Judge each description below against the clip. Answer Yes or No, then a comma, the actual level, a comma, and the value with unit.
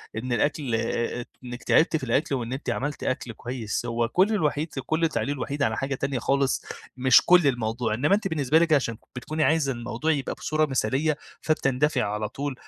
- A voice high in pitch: No, low, 135 Hz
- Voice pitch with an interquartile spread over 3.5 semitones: Yes, average, 4.0 semitones